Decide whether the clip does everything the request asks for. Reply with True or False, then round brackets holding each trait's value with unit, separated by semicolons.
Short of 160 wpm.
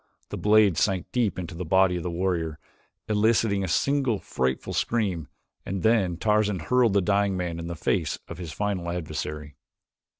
False (170 wpm)